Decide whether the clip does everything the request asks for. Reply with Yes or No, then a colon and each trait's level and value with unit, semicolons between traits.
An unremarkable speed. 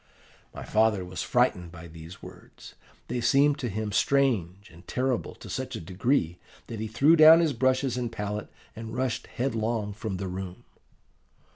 Yes: average, 165 wpm